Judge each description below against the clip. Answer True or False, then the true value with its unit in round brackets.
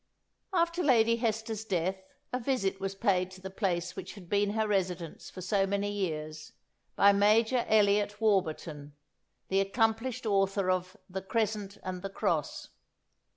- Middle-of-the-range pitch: False (200 Hz)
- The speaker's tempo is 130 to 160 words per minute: True (155 wpm)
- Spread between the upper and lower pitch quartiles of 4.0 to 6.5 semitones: False (2.9 semitones)